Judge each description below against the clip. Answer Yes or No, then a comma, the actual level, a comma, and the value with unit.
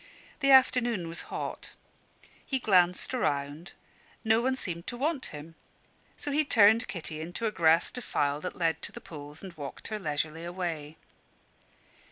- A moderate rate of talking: Yes, average, 155 wpm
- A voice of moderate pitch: Yes, medium, 175 Hz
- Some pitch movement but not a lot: No, wide, 6.9 semitones